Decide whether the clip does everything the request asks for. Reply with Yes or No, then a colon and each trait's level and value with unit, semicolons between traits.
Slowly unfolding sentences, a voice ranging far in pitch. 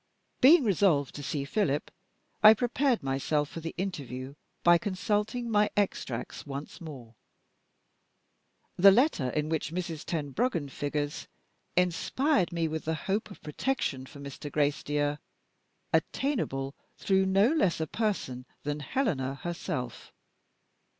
Yes: slow, 125 wpm; wide, 6.3 semitones